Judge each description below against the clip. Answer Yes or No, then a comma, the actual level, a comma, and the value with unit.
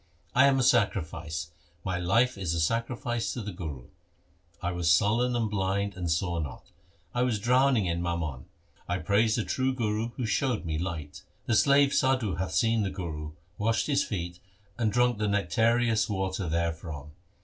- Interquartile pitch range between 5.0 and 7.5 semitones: Yes, wide, 5.6 semitones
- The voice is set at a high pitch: No, low, 100 Hz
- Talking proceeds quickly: No, average, 175 wpm